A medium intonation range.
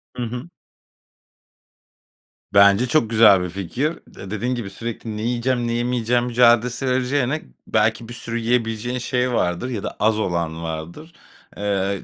Yes: average, 3.5 semitones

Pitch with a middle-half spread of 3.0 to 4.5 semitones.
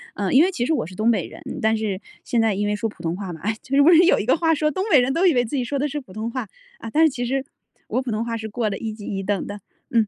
No: average, 5.0 semitones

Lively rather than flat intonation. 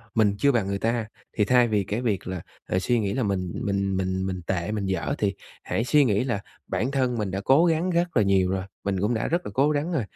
No: average, 4.7 semitones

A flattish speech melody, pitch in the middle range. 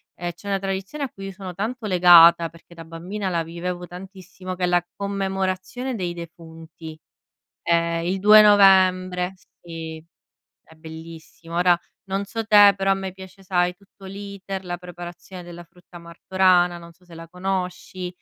Yes: narrow, 2.1 semitones; medium, 180 Hz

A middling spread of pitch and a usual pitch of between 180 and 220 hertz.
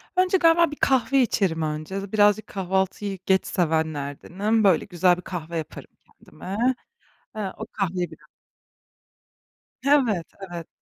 Yes: average, 4.2 semitones; high, 190 Hz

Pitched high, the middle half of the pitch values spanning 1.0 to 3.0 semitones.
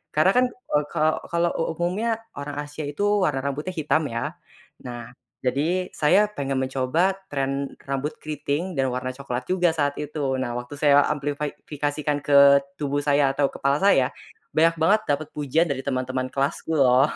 No: medium, 145 Hz; average, 2.7 semitones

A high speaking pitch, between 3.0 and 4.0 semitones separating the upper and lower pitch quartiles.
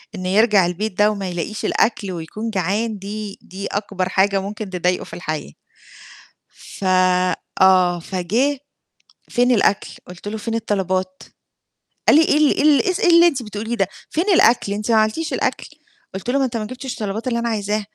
Yes: high, 210 Hz; average, 3.7 semitones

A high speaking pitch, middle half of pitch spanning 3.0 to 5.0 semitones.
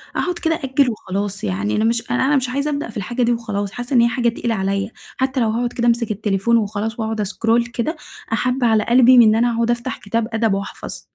No: high, 230 Hz; narrow, 2.5 semitones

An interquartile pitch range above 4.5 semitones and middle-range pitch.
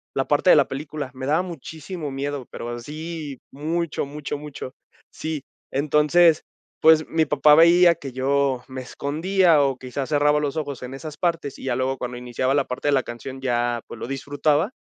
No: average, 2.9 semitones; medium, 145 Hz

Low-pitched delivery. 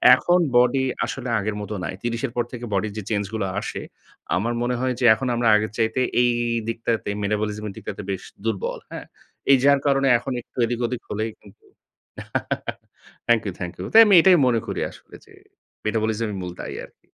Yes: low, 115 Hz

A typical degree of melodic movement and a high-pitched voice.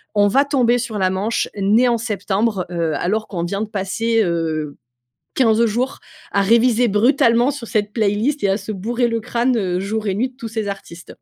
Yes: average, 3.3 semitones; high, 215 Hz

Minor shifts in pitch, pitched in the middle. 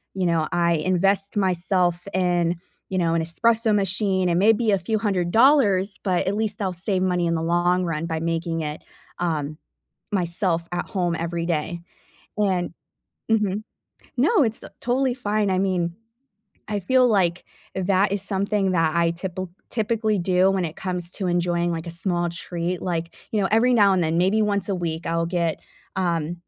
No: average, 3.0 semitones; medium, 180 Hz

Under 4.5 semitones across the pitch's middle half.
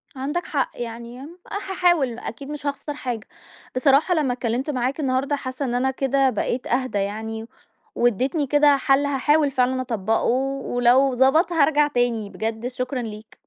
Yes: average, 3.0 semitones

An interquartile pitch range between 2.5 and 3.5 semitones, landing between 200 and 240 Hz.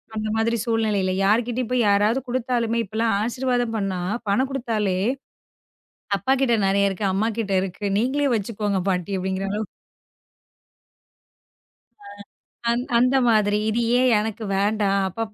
Yes: average, 3.0 semitones; high, 220 Hz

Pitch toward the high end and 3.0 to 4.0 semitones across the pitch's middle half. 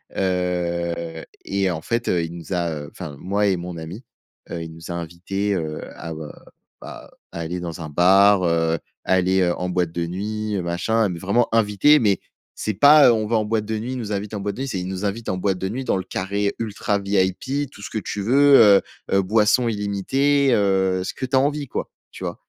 No: low, 100 Hz; average, 3.7 semitones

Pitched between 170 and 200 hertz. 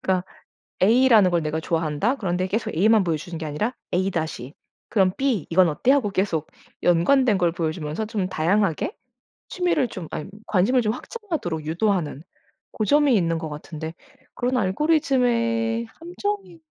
Yes: high, 195 Hz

